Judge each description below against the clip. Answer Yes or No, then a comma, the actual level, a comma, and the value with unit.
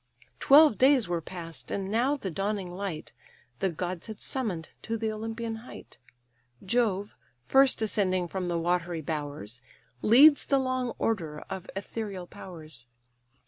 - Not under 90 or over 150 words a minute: Yes, average, 140 wpm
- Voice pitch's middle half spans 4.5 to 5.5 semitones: Yes, average, 4.8 semitones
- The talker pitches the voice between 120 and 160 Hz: No, high, 195 Hz